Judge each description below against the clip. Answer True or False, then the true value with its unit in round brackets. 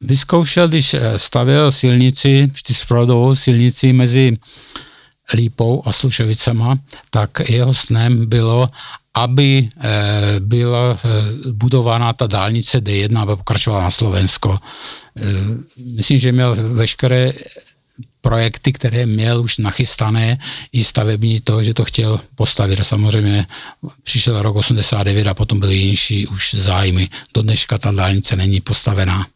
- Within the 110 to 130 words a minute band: True (115 wpm)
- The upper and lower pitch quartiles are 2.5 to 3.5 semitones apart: True (3.0 semitones)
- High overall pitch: False (115 Hz)